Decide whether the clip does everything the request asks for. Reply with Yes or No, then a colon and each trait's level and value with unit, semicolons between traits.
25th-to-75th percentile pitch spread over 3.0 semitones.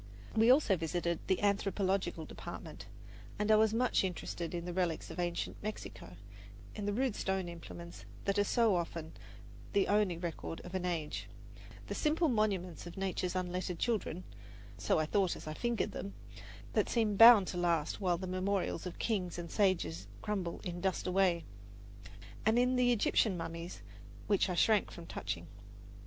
Yes: average, 3.4 semitones